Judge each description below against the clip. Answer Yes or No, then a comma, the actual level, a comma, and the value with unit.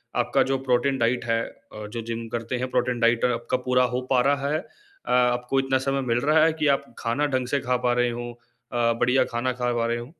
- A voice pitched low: Yes, low, 125 Hz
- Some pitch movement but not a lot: No, narrow, 2.1 semitones